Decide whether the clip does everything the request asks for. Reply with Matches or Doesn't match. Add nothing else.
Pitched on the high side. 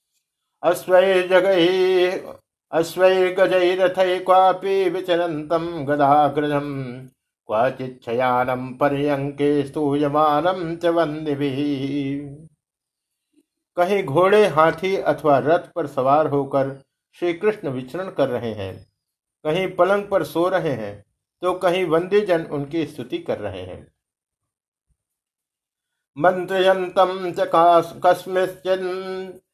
Doesn't match